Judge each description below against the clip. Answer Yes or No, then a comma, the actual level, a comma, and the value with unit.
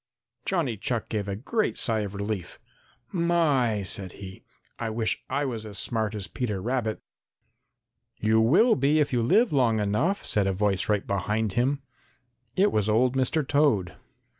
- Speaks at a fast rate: No, average, 165 wpm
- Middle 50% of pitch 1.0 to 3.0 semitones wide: No, average, 5.0 semitones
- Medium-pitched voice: No, low, 110 Hz